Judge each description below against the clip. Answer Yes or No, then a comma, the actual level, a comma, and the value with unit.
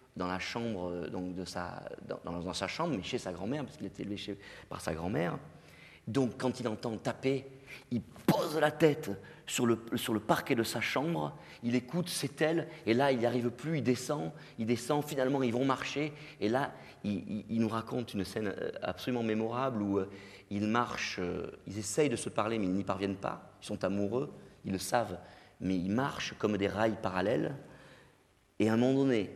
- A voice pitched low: Yes, low, 115 Hz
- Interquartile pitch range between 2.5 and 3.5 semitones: No, average, 4.8 semitones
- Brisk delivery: No, average, 205 wpm